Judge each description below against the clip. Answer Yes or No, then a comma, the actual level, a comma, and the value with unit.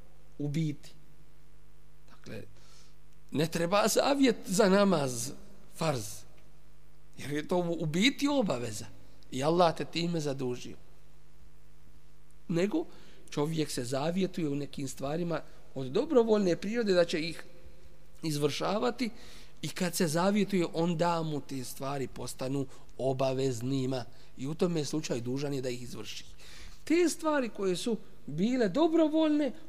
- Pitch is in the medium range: Yes, medium, 155 Hz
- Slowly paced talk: Yes, slow, 120 wpm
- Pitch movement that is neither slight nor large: No, wide, 5.8 semitones